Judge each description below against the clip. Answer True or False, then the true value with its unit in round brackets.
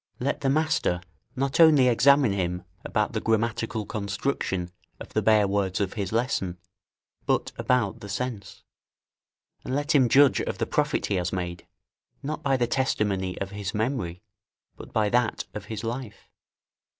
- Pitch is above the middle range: False (110 Hz)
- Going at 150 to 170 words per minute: True (160 wpm)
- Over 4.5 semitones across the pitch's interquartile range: True (4.9 semitones)